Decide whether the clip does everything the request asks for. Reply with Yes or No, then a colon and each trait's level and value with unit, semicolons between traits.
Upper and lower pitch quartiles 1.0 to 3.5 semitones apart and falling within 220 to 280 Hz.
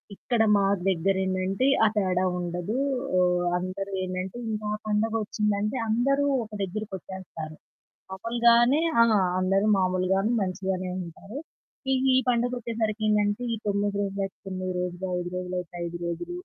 No: average, 2.8 semitones; high, 195 Hz